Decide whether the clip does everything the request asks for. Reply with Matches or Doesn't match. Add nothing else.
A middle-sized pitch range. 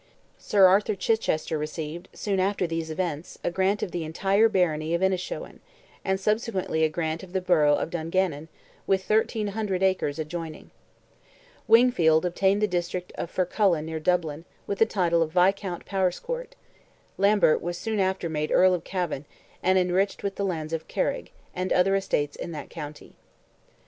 Matches